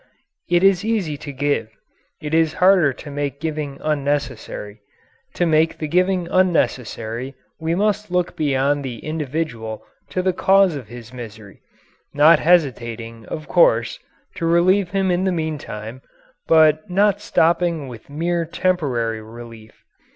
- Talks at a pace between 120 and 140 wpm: Yes, slow, 135 wpm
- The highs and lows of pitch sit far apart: Yes, wide, 5.7 semitones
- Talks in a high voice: No, medium, 155 Hz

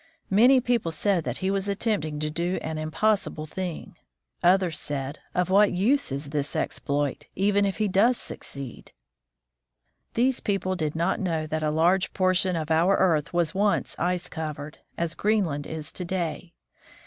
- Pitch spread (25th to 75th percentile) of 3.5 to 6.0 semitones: Yes, average, 4.2 semitones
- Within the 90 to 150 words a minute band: No, average, 170 wpm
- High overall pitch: No, medium, 175 Hz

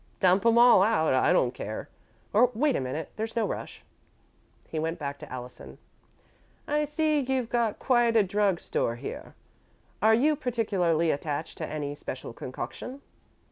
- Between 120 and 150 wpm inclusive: No, average, 160 wpm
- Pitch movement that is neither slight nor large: No, wide, 7.9 semitones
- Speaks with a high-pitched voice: Yes, high, 200 Hz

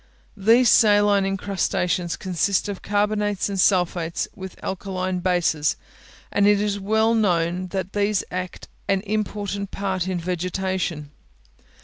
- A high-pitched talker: Yes, high, 195 Hz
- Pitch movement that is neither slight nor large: No, narrow, 2.2 semitones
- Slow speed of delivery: Yes, slow, 115 wpm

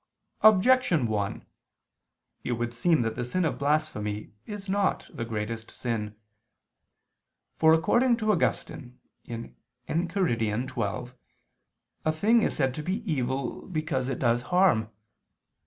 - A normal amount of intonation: No, wide, 7.7 semitones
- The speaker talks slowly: Yes, slow, 125 wpm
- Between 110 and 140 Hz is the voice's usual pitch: Yes, low, 135 Hz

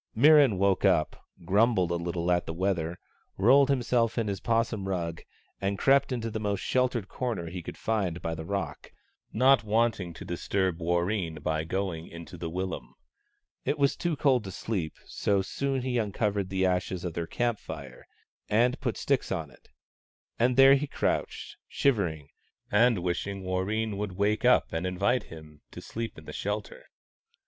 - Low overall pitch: Yes, low, 100 Hz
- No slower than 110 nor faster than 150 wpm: No, average, 170 wpm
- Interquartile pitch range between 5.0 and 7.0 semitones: Yes, average, 5.3 semitones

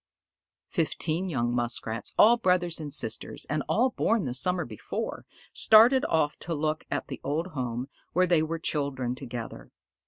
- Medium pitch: Yes, medium, 155 Hz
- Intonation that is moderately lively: No, wide, 6.2 semitones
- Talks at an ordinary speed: Yes, average, 155 wpm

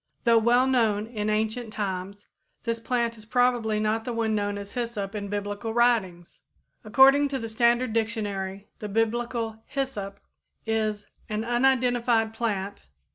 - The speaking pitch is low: No, high, 225 Hz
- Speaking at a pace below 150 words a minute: Yes, average, 140 wpm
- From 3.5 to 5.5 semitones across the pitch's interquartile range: No, narrow, 2.5 semitones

